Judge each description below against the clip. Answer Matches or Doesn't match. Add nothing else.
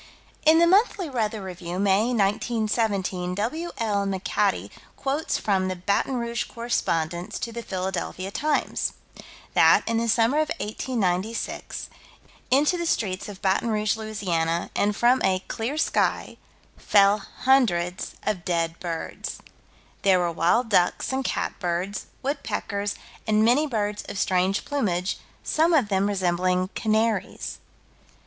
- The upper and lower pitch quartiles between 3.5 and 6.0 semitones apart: Matches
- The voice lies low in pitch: Doesn't match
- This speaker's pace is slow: Matches